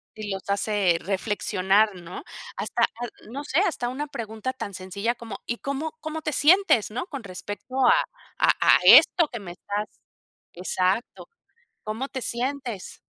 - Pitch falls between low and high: No, high, 225 Hz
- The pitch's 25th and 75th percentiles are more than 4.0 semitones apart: Yes, average, 5.2 semitones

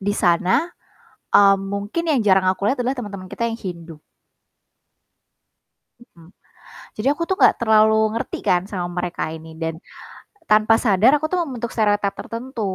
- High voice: Yes, high, 210 Hz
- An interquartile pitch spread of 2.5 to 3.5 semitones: No, average, 4.0 semitones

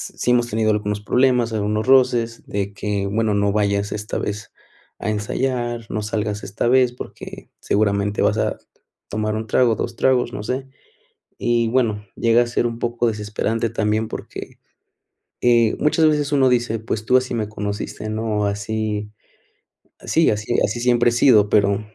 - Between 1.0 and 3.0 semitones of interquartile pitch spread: Yes, narrow, 2.4 semitones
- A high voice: No, low, 110 Hz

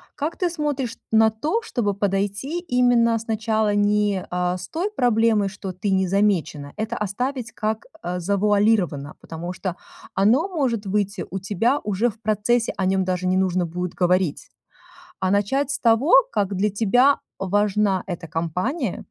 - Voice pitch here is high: Yes, high, 205 Hz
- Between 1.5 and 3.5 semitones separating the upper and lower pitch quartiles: No, average, 3.9 semitones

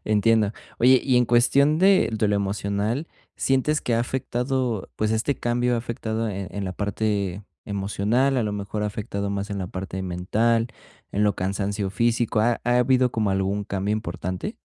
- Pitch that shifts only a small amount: No, average, 3.2 semitones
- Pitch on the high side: No, low, 110 Hz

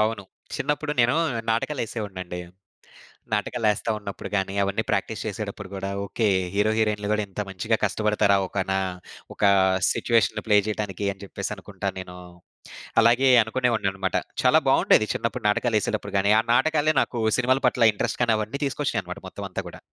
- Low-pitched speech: Yes, low, 105 Hz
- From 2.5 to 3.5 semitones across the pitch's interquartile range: Yes, average, 2.8 semitones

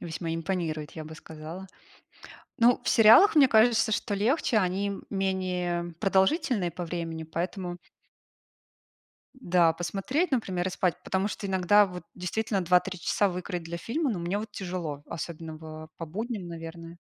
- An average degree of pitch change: Yes, average, 3.7 semitones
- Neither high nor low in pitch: Yes, medium, 180 Hz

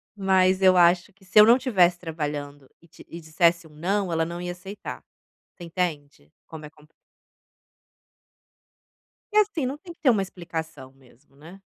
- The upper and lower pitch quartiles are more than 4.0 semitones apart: No, average, 3.7 semitones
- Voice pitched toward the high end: No, medium, 175 Hz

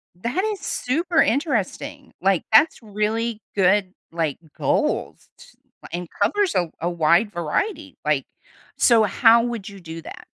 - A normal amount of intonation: No, wide, 6.7 semitones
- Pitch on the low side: No, high, 215 Hz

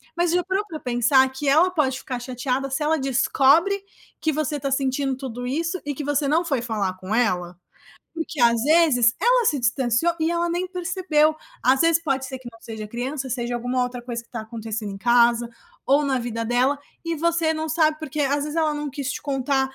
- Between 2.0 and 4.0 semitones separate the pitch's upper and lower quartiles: No, average, 4.5 semitones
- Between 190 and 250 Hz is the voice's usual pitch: No, very high, 275 Hz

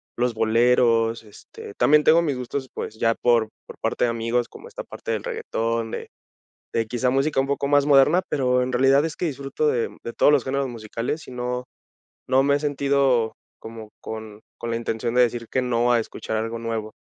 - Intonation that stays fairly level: No, average, 3.2 semitones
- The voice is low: Yes, low, 125 Hz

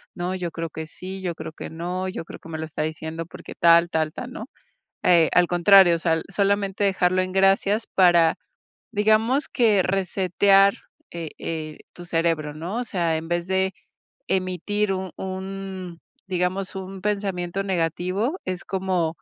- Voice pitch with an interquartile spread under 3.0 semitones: Yes, narrow, 2.6 semitones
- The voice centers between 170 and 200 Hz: Yes, medium, 185 Hz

